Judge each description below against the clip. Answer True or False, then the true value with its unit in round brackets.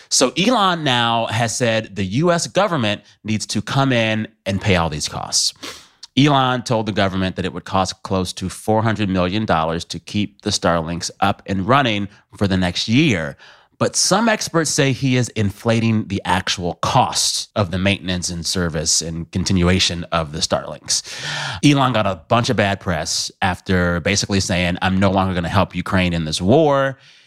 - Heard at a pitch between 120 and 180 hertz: False (100 Hz)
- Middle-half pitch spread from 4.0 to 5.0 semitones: True (4.7 semitones)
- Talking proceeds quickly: False (175 wpm)